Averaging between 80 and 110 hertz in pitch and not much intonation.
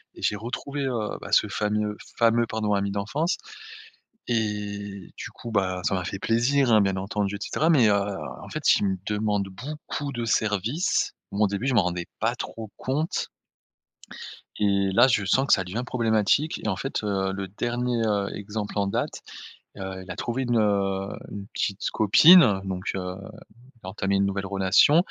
No: low, 105 Hz; average, 3.2 semitones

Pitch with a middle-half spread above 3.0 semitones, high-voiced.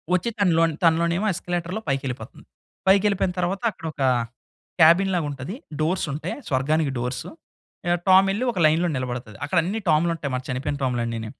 No: average, 4.9 semitones; medium, 165 Hz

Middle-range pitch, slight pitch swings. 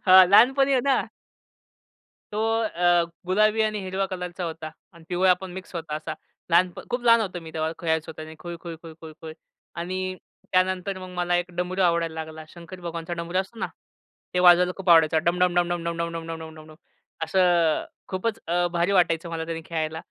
Yes: medium, 175 Hz; narrow, 2.1 semitones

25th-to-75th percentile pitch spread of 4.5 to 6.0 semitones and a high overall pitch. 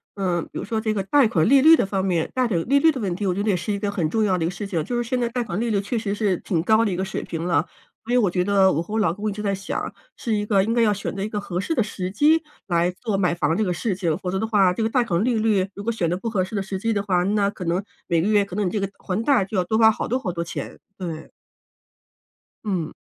No: average, 3.5 semitones; high, 200 Hz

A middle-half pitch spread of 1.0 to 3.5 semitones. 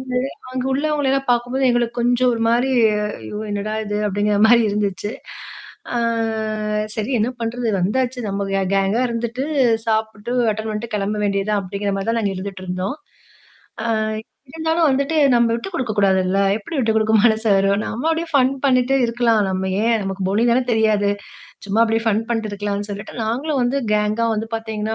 Yes: average, 3.2 semitones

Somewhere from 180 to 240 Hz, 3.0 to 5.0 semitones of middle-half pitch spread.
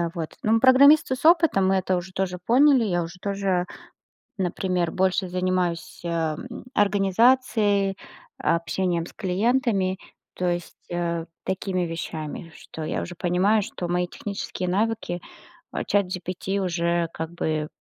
No: medium, 185 Hz; narrow, 2.6 semitones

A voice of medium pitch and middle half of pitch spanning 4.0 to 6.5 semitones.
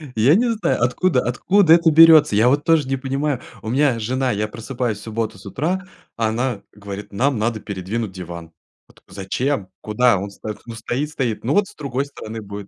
No: low, 120 Hz; average, 5.2 semitones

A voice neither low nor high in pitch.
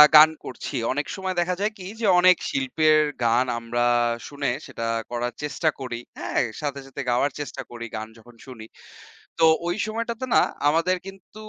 Yes: medium, 145 Hz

